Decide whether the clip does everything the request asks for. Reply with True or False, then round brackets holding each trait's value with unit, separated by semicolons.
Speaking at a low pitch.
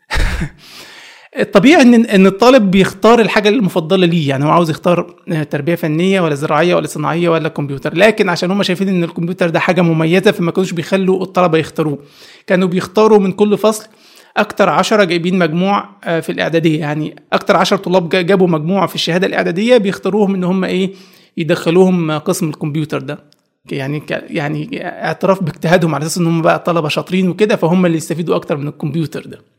False (180 Hz)